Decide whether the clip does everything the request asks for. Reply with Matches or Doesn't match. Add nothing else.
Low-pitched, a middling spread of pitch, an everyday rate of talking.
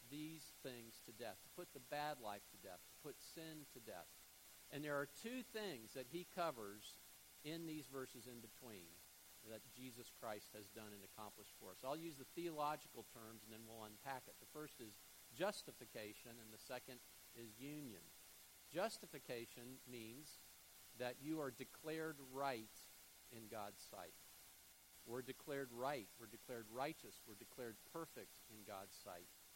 Doesn't match